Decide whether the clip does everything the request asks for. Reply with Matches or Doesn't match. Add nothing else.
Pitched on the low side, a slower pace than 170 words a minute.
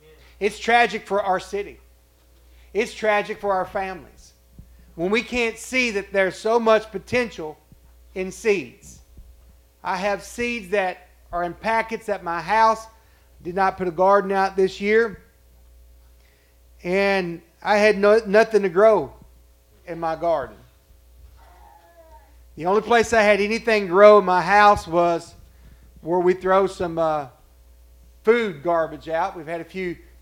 Doesn't match